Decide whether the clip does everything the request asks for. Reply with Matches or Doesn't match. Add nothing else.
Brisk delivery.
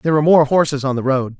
Matches